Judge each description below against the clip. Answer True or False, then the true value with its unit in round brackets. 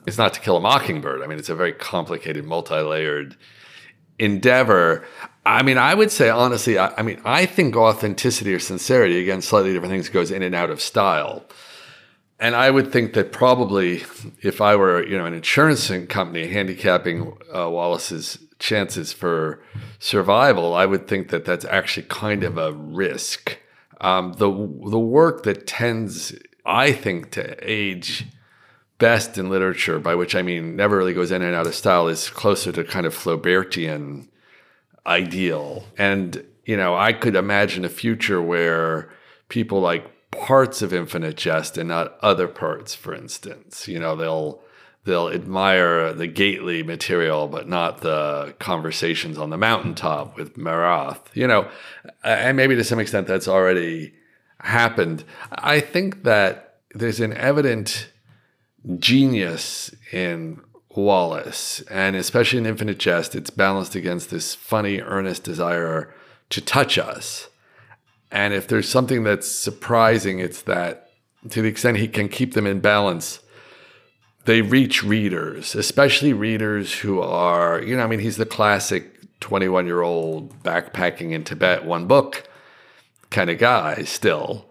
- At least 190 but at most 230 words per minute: False (150 wpm)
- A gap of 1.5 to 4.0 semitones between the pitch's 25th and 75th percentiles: False (4.7 semitones)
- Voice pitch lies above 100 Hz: False (95 Hz)